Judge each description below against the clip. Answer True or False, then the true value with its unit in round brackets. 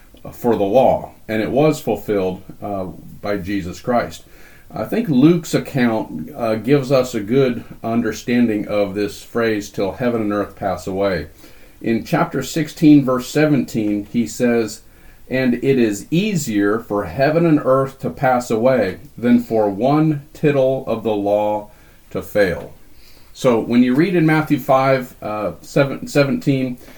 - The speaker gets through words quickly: False (150 wpm)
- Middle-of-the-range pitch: False (120 Hz)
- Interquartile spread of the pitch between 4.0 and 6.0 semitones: True (4.6 semitones)